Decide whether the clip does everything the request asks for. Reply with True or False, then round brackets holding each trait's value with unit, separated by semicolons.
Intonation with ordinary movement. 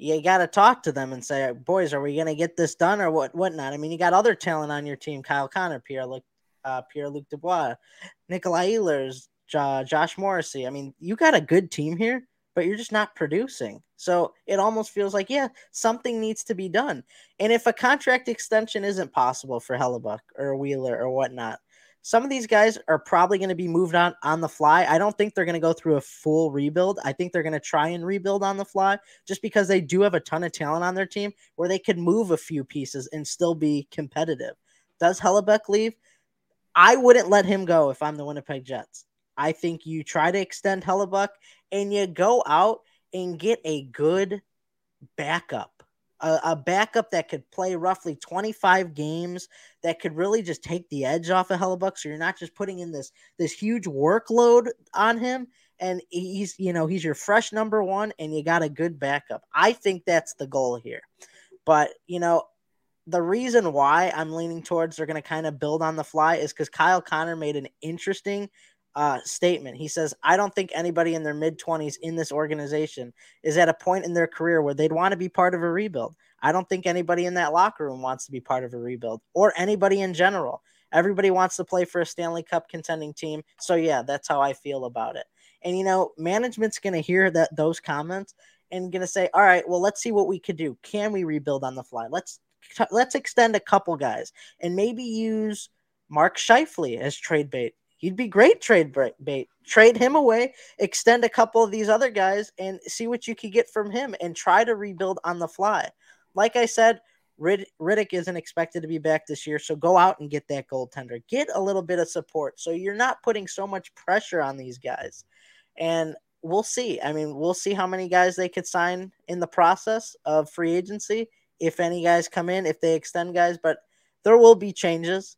True (4.4 semitones)